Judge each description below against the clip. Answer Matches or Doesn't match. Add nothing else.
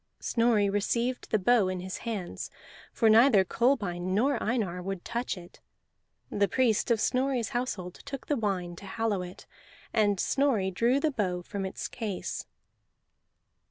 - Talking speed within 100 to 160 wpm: Matches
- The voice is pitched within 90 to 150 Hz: Doesn't match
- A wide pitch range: Doesn't match